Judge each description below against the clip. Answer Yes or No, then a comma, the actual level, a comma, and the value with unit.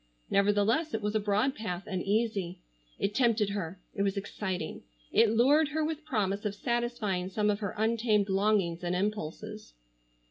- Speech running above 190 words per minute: No, average, 165 wpm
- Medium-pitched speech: No, high, 210 Hz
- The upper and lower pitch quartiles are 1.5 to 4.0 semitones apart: Yes, average, 2.8 semitones